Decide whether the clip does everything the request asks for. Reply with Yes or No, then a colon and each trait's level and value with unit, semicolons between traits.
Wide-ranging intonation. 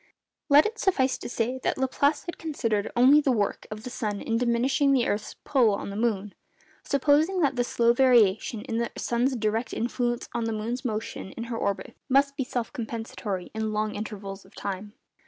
No: average, 3.6 semitones